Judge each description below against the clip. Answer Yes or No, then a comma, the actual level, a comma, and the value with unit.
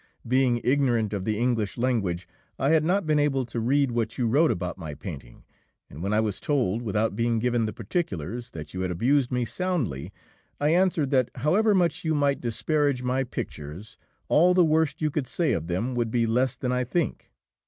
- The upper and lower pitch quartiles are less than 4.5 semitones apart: No, average, 5.1 semitones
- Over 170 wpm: Yes, average, 200 wpm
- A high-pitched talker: No, low, 125 Hz